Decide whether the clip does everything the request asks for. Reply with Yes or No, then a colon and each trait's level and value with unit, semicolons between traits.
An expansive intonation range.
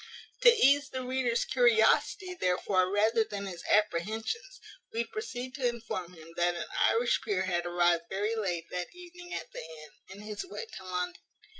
Yes: wide, 6.2 semitones